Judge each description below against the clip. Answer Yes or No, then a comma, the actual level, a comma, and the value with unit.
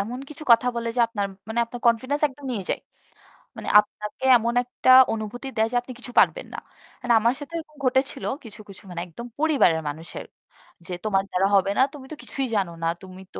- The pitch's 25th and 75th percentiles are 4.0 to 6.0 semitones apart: Yes, average, 4.7 semitones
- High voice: Yes, high, 235 Hz